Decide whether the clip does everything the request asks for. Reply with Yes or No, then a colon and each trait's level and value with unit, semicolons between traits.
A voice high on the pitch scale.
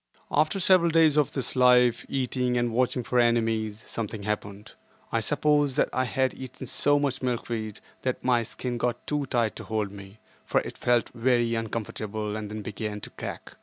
No: low, 120 Hz